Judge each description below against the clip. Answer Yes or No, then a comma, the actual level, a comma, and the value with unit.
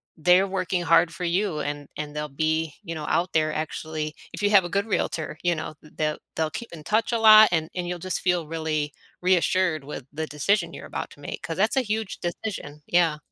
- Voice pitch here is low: No, medium, 165 Hz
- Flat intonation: No, average, 3.3 semitones